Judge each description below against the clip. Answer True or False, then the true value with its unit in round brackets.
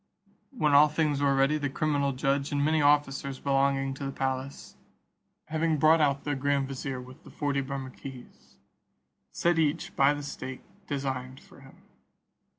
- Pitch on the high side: False (140 Hz)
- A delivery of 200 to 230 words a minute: False (155 wpm)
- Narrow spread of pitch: True (1.5 semitones)